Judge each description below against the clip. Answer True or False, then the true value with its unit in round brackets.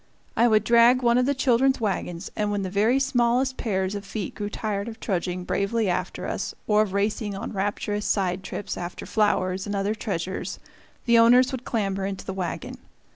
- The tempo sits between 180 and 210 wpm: True (190 wpm)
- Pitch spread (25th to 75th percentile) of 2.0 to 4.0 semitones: True (3.4 semitones)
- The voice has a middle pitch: False (210 Hz)